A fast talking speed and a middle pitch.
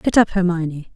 No: average, 190 wpm; medium, 175 Hz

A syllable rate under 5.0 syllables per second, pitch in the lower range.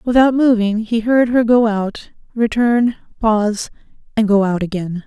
No: 4.5 syllables/s; high, 220 Hz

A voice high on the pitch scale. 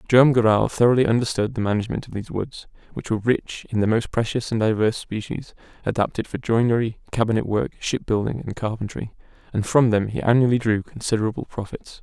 No: low, 115 Hz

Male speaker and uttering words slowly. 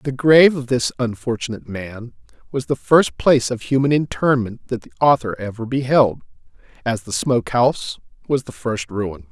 No: male; average, 165 wpm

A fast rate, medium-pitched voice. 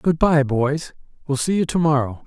No: average, 160 wpm; medium, 145 Hz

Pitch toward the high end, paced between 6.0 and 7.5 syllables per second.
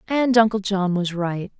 No: high, 200 Hz; 4.3 syllables/s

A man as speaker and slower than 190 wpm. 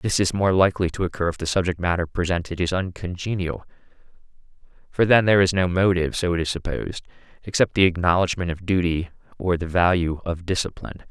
Yes: male; average, 180 wpm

